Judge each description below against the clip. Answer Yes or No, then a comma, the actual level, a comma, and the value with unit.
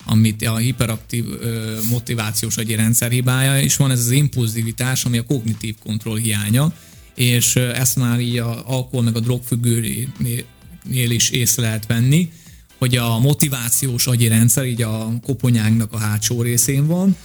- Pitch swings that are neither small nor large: No, narrow, 2.2 semitones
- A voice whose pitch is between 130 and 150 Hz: No, low, 120 Hz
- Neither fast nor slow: Yes, average, 140 wpm